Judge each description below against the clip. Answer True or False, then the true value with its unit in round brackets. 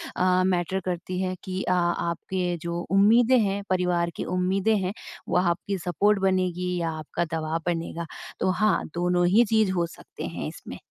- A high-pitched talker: False (180 Hz)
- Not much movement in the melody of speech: True (1.9 semitones)